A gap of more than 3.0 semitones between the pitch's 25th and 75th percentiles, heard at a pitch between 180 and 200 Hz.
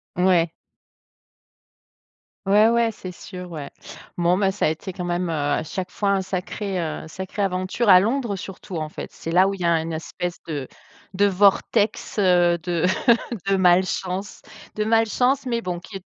No: narrow, 2.6 semitones; medium, 185 Hz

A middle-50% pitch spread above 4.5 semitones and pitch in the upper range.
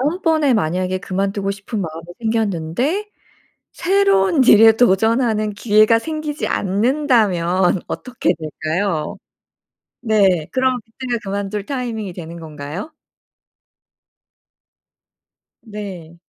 Yes: wide, 5.5 semitones; high, 210 Hz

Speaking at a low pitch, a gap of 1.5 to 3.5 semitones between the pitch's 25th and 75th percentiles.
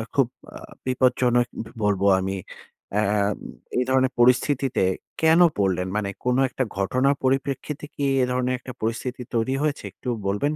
No: low, 125 Hz; average, 4.1 semitones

